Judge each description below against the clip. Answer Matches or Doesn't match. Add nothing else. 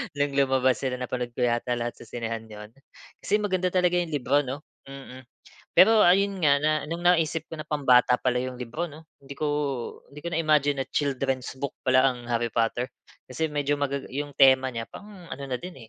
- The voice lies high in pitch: Doesn't match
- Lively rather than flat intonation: Doesn't match